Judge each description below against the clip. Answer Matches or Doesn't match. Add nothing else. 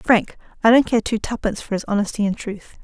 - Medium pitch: Doesn't match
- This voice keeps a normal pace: Doesn't match